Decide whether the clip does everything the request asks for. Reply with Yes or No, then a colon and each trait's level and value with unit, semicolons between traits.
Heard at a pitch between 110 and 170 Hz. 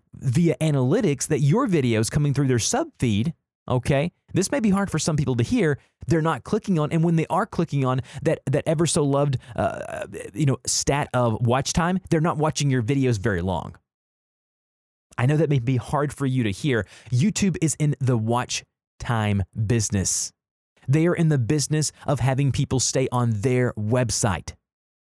Yes: low, 135 Hz